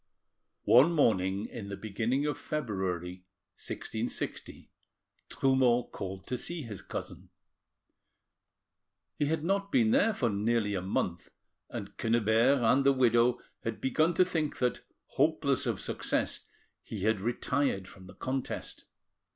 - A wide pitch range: Yes, wide, 5.9 semitones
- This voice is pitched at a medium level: No, low, 120 Hz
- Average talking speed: No, slow, 130 wpm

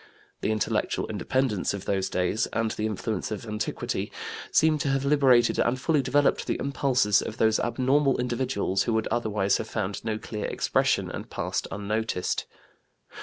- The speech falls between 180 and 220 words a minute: No, average, 160 wpm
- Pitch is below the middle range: Yes, low, 110 Hz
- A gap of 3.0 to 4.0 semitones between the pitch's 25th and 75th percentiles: Yes, average, 3.7 semitones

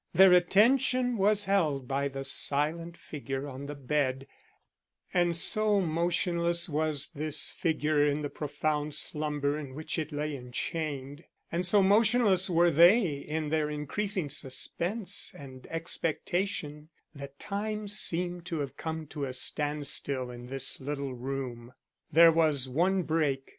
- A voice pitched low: No, medium, 155 Hz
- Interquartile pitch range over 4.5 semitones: No, average, 3.8 semitones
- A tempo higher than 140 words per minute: No, slow, 135 wpm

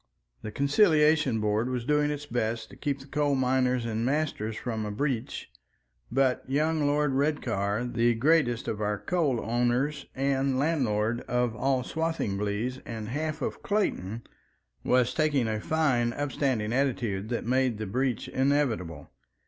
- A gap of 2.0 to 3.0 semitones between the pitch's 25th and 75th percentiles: No, average, 4.3 semitones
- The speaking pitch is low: Yes, low, 125 Hz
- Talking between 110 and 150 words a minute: Yes, average, 140 wpm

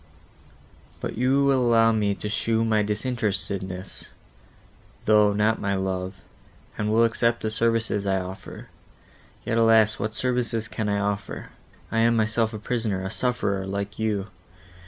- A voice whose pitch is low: Yes, low, 110 Hz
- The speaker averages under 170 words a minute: Yes, average, 145 wpm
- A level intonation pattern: Yes, narrow, 2.3 semitones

